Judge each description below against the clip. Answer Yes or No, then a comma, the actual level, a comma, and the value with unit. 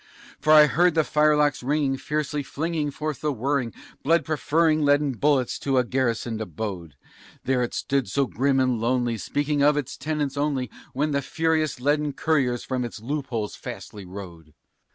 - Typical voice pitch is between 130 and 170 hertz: Yes, medium, 140 Hz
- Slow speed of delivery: No, average, 165 wpm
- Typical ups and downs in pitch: Yes, average, 3.6 semitones